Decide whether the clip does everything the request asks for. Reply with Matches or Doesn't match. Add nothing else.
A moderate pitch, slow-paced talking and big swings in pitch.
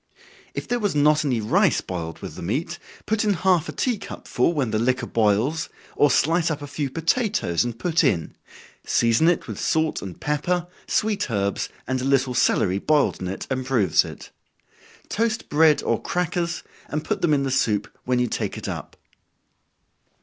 Doesn't match